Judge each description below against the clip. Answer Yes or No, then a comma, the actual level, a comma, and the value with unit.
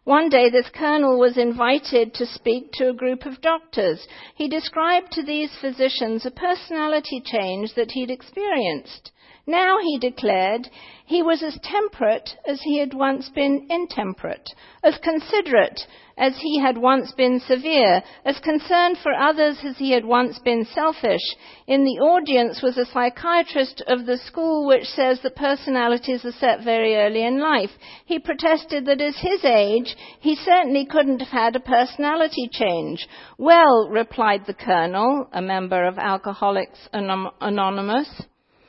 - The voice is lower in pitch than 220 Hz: No, very high, 265 Hz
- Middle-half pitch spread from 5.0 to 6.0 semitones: No, average, 4.2 semitones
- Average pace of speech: Yes, average, 150 wpm